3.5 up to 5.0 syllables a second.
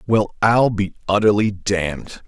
Yes: 4.1 syllables/s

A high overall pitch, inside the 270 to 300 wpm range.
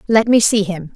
No: high, 205 Hz; fast, 250 wpm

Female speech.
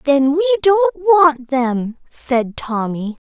Yes: female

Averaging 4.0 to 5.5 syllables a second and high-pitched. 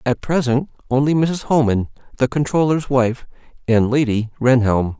No: 4.6 syllables/s; low, 130 Hz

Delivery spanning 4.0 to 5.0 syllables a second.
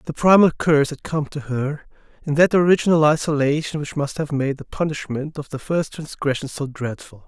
No: 5.4 syllables/s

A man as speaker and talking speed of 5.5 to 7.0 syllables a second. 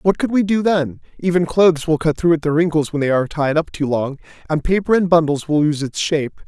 Yes: male; 5.9 syllables/s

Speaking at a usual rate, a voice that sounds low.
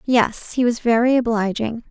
No: average, 155 wpm; high, 235 Hz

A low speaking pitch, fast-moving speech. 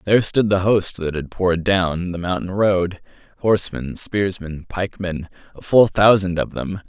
No: very low, 90 Hz; average, 155 wpm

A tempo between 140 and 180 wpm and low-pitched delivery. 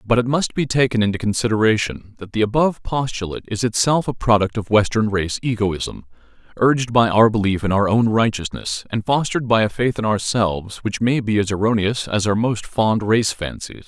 No: average, 195 wpm; low, 110 Hz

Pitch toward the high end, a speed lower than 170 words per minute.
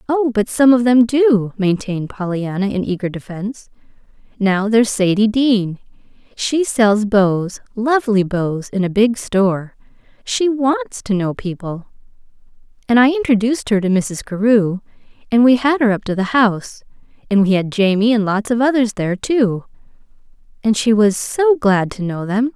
Yes: high, 220 Hz; average, 160 wpm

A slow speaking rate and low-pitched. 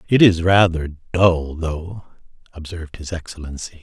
Yes: slow, 125 wpm; very low, 85 Hz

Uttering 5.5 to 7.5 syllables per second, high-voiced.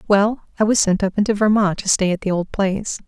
Yes: 5.9 syllables/s; high, 200 Hz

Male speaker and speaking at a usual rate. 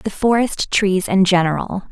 No: female; average, 155 wpm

